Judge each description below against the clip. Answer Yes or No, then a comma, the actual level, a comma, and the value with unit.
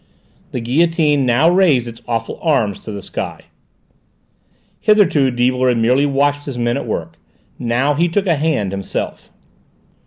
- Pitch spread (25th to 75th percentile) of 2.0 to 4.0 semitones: No, average, 4.7 semitones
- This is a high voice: No, low, 130 Hz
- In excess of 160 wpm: No, average, 150 wpm